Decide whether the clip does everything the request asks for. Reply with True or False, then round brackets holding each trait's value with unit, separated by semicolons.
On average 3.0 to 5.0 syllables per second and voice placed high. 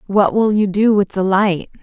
True (4.5 syllables/s; 200 Hz)